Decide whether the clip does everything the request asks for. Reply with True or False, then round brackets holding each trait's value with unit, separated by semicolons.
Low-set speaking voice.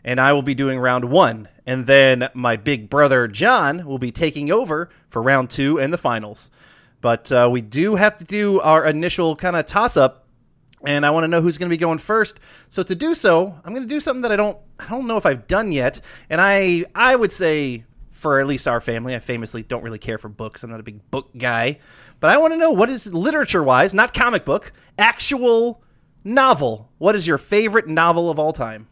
False (150 Hz)